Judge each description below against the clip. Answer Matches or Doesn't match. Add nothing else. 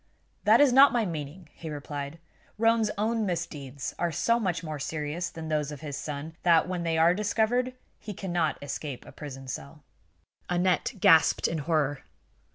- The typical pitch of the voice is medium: Matches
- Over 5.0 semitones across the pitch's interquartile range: Matches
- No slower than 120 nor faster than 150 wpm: Doesn't match